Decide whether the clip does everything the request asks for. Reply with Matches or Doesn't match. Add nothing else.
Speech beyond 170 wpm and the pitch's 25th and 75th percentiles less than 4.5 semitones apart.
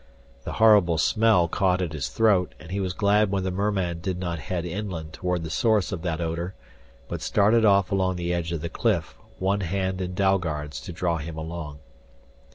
Matches